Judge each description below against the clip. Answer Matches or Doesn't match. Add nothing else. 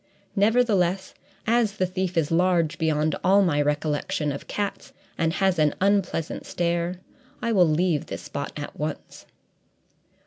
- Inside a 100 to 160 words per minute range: Matches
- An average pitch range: Matches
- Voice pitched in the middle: Matches